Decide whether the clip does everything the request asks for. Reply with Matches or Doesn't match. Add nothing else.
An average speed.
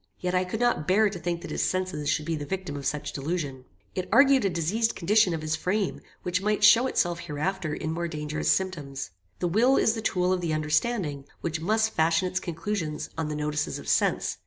Doesn't match